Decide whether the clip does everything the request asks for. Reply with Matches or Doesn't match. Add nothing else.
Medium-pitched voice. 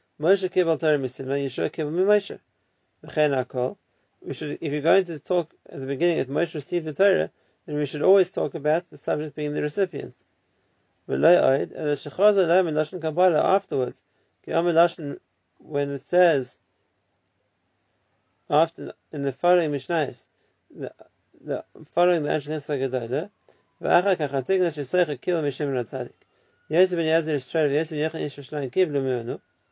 Matches